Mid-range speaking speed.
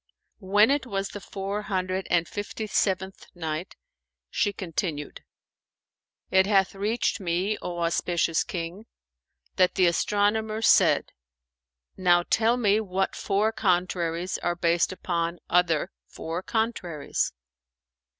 No: slow, 115 wpm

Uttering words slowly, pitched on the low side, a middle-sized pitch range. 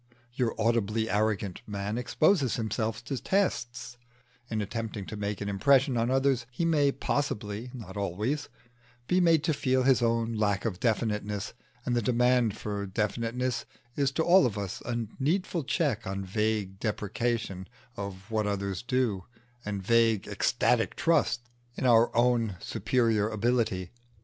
No: average, 145 wpm; low, 115 Hz; average, 3.5 semitones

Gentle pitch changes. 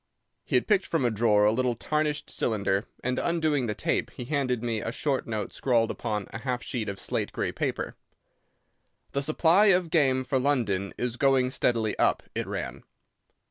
No: average, 4.3 semitones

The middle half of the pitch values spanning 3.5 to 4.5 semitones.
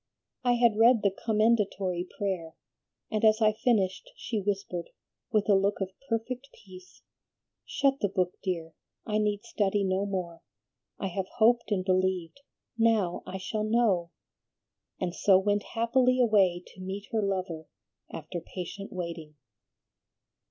No: average, 3.1 semitones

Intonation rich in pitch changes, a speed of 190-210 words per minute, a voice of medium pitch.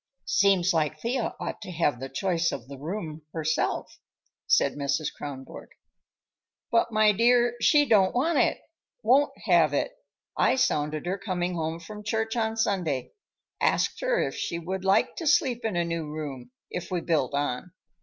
No: wide, 6.4 semitones; average, 165 wpm; medium, 180 Hz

